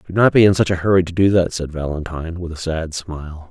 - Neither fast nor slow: No, fast, 275 wpm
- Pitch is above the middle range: No, very low, 85 Hz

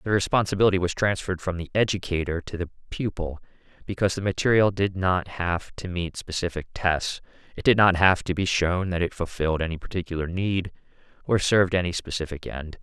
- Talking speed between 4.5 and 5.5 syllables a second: No, 5.8 syllables/s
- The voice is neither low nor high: No, very low, 90 Hz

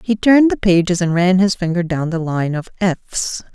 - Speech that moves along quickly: Yes, fast, 220 wpm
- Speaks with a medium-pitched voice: Yes, medium, 180 Hz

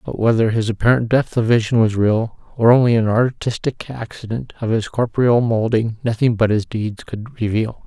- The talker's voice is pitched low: Yes, low, 115 Hz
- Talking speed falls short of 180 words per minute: No, average, 185 wpm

